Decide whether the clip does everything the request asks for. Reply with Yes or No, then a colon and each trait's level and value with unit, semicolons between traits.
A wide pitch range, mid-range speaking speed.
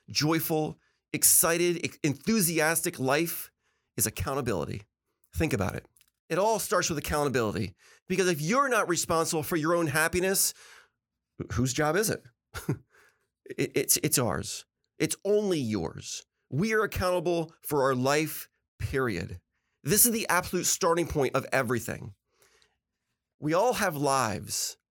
No: wide, 5.9 semitones; slow, 130 wpm